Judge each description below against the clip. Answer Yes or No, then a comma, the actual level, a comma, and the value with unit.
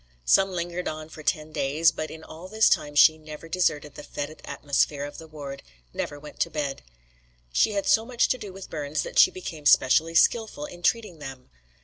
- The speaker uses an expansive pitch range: No, average, 3.5 semitones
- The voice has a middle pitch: Yes, medium, 155 Hz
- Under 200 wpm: No, fast, 205 wpm